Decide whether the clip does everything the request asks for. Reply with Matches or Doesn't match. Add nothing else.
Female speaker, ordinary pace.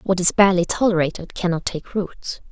Matches